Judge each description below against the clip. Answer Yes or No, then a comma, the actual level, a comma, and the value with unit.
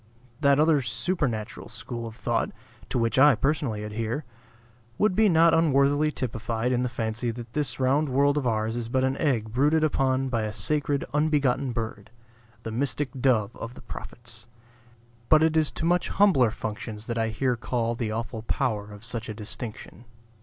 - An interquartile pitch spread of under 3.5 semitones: No, average, 4.2 semitones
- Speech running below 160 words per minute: No, average, 175 wpm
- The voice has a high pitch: No, low, 125 Hz